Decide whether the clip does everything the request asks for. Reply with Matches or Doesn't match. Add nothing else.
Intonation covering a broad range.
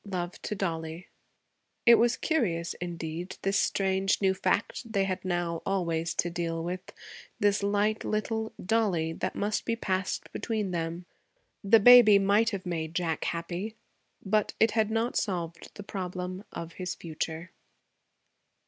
Doesn't match